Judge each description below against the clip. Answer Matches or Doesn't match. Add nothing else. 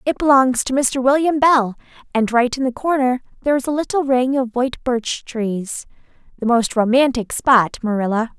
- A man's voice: Doesn't match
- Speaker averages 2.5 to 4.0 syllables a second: Doesn't match